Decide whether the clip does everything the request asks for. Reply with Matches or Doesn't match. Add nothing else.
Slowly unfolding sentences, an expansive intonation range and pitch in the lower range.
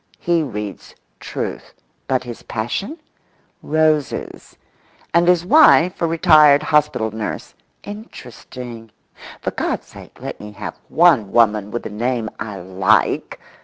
Matches